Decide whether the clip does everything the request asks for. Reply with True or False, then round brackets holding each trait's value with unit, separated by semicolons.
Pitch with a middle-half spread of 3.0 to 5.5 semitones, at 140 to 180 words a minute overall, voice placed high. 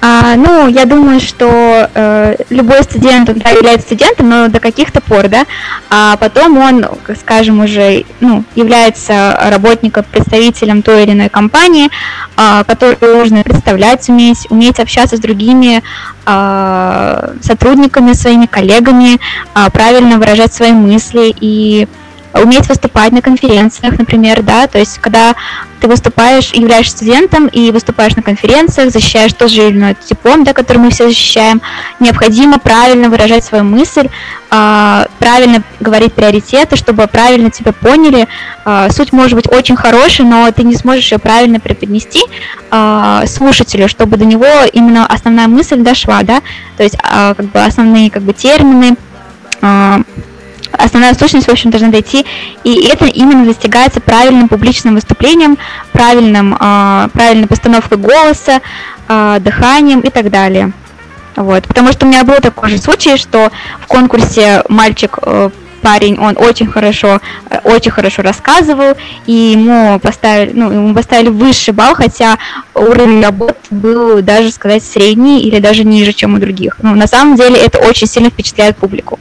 False (2.6 semitones; 150 wpm; 230 Hz)